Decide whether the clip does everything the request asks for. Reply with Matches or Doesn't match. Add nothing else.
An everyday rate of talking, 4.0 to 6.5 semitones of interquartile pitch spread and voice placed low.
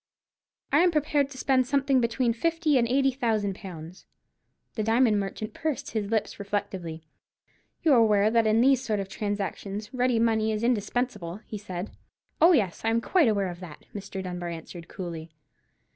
Doesn't match